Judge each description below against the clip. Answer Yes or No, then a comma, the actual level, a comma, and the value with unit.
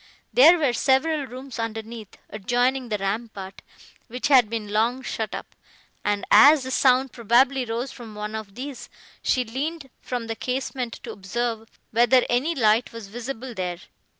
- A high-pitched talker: Yes, high, 240 Hz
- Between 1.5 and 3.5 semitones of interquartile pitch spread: Yes, average, 3.1 semitones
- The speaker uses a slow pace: No, average, 155 wpm